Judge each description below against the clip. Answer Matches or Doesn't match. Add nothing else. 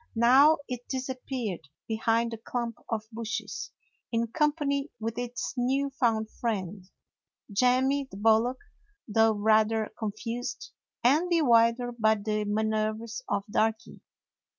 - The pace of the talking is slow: Matches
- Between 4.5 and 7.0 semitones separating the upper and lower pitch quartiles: Doesn't match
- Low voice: Doesn't match